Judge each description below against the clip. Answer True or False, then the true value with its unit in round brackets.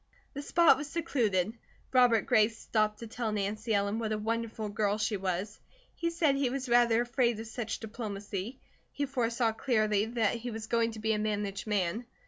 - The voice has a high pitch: True (225 Hz)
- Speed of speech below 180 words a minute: False (185 wpm)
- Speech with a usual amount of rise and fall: False (2.3 semitones)